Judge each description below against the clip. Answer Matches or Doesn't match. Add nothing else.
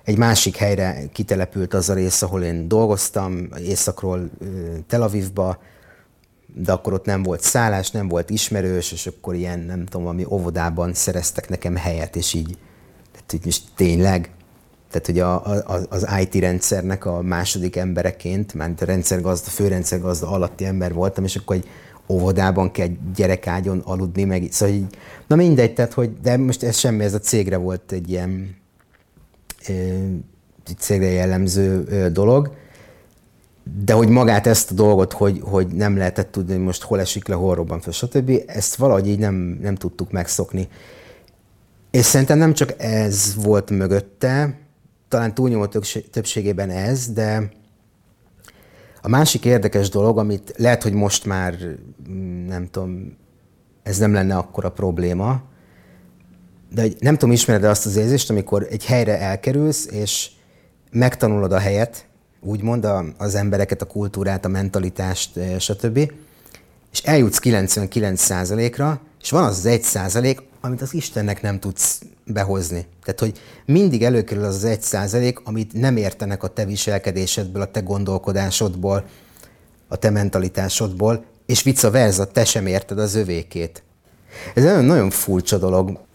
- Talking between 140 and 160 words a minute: Matches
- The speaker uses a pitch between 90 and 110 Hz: Matches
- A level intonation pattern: Doesn't match